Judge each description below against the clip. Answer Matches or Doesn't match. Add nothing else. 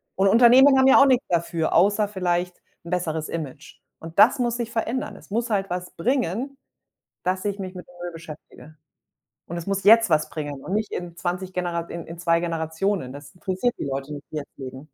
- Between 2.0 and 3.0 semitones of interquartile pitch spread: Doesn't match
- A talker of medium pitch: Matches